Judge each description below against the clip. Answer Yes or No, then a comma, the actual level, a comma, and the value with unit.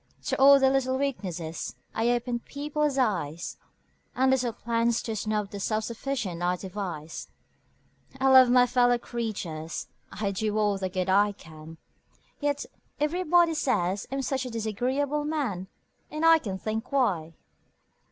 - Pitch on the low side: No, high, 230 Hz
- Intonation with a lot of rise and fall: Yes, wide, 5.8 semitones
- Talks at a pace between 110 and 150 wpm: Yes, average, 145 wpm